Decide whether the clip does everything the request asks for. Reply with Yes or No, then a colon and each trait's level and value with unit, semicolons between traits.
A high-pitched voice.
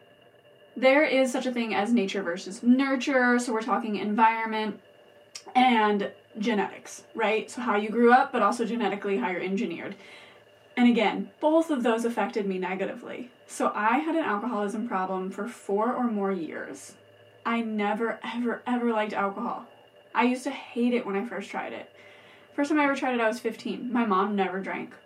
Yes: high, 220 Hz